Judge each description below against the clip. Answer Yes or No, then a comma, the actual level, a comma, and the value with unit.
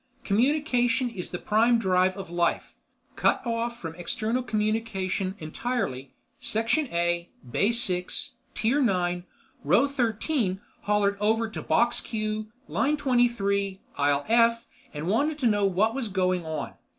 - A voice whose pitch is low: No, high, 215 Hz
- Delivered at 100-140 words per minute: Yes, slow, 135 wpm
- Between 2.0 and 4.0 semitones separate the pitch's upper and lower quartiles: No, average, 4.4 semitones